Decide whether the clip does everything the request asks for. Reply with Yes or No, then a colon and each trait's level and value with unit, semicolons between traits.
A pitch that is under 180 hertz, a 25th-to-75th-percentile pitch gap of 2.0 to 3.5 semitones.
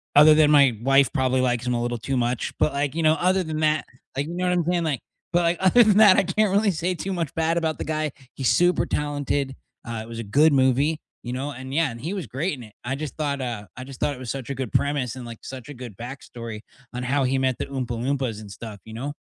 No: medium, 140 Hz; average, 4.2 semitones